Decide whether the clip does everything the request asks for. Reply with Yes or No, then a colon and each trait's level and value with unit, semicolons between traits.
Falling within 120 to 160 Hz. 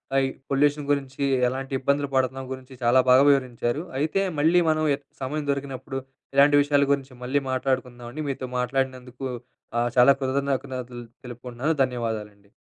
Yes: low, 135 Hz